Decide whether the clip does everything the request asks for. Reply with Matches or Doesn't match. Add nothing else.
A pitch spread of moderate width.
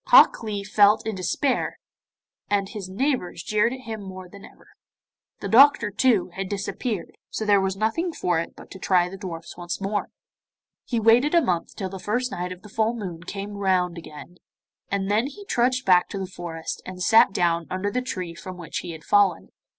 Matches